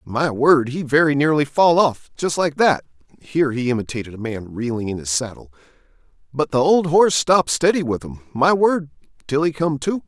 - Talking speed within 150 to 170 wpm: No, average, 190 wpm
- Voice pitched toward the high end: No, medium, 140 Hz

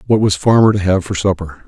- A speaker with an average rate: No, fast, 250 wpm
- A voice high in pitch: No, very low, 95 Hz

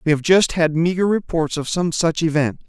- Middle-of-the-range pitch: Yes, medium, 165 Hz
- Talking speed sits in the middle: No, fast, 225 wpm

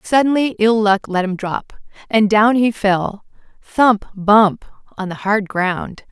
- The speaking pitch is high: Yes, high, 210 Hz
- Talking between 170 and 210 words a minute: No, slow, 135 wpm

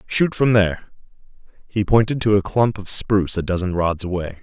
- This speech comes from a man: Yes, male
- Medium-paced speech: Yes, average, 190 wpm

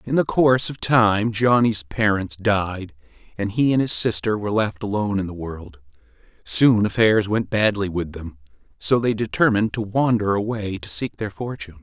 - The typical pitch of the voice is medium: No, low, 105 Hz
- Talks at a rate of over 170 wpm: Yes, average, 180 wpm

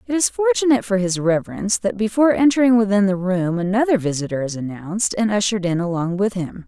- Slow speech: No, average, 200 wpm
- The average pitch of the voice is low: No, high, 205 Hz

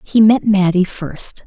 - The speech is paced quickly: No, average, 165 wpm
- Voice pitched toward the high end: Yes, high, 195 Hz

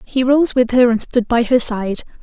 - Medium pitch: No, high, 240 Hz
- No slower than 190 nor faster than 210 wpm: No, fast, 245 wpm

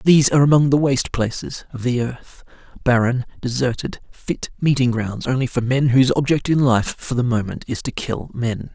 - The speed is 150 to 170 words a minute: No, average, 185 wpm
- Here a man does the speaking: Yes, male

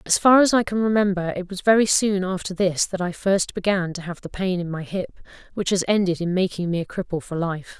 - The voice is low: No, medium, 185 Hz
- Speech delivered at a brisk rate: Yes, fast, 255 wpm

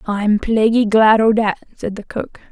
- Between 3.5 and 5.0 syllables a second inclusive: Yes, 4.3 syllables/s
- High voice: Yes, high, 215 Hz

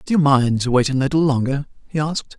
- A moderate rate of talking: No, fast, 225 wpm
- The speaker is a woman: No, male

